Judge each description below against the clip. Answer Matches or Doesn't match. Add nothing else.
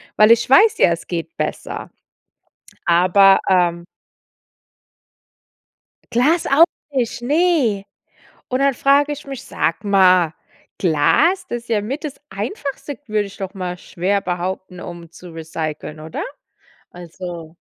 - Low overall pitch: Doesn't match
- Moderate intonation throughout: Doesn't match